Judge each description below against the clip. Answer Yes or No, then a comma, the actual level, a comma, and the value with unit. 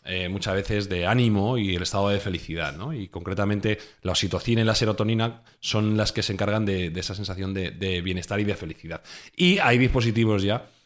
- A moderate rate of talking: No, fast, 205 wpm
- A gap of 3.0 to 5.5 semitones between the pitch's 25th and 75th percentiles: No, narrow, 2.5 semitones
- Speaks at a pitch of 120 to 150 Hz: No, low, 100 Hz